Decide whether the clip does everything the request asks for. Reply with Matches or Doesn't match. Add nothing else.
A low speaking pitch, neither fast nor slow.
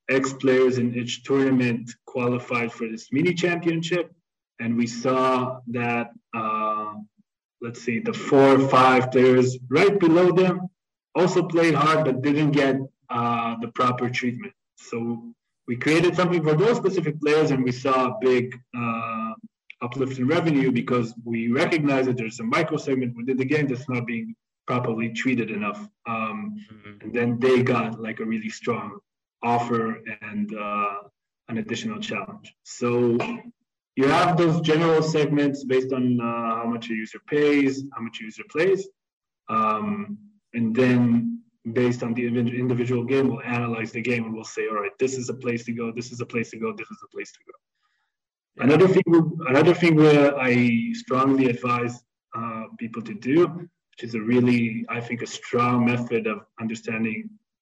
Matches